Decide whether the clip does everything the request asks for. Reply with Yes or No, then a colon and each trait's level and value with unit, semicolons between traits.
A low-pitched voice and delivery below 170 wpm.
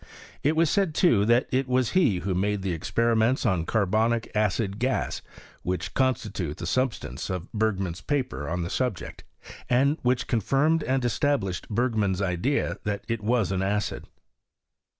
Yes: low, 110 Hz; average, 155 wpm